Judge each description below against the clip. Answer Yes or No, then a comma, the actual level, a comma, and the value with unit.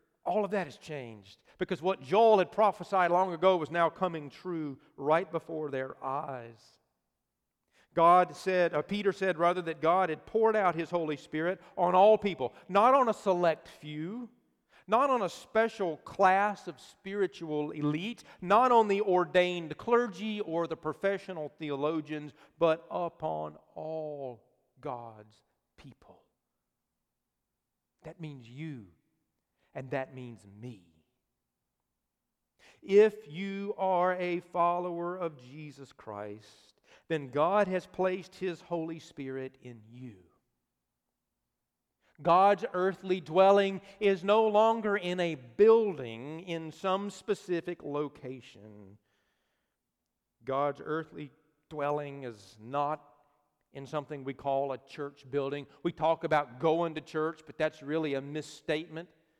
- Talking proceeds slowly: Yes, slow, 125 wpm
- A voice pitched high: No, medium, 160 Hz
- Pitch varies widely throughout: No, average, 4.9 semitones